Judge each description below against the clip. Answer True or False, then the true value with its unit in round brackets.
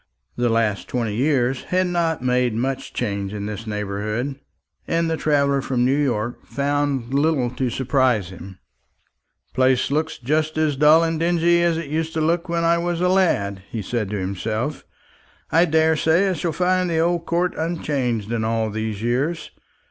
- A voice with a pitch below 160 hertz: True (140 Hz)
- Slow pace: False (175 wpm)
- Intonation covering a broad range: True (6.1 semitones)